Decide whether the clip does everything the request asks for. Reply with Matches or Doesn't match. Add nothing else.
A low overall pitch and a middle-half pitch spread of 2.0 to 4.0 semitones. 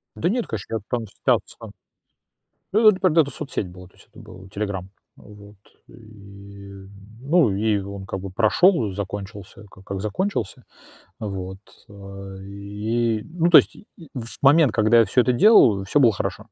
Doesn't match